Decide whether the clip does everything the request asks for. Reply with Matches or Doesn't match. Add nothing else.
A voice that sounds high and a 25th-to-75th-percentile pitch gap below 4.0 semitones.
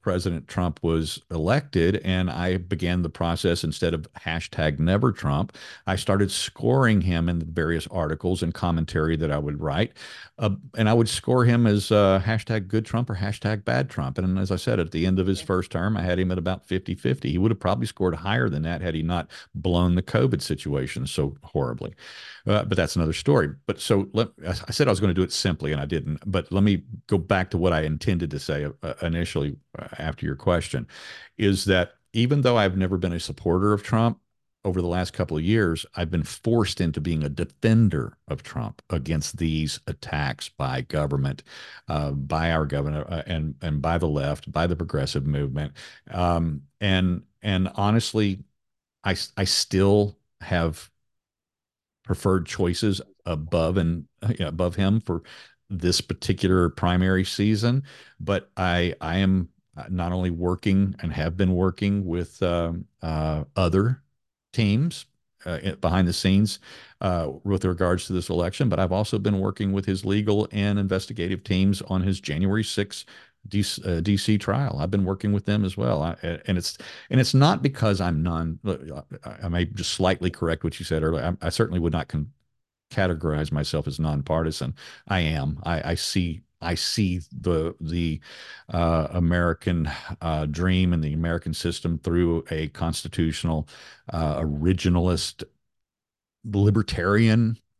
Doesn't match